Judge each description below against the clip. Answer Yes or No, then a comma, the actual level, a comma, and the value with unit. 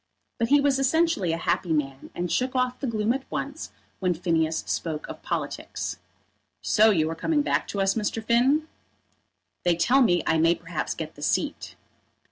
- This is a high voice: Yes, high, 210 Hz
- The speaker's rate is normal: Yes, average, 180 wpm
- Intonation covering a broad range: Yes, wide, 7.9 semitones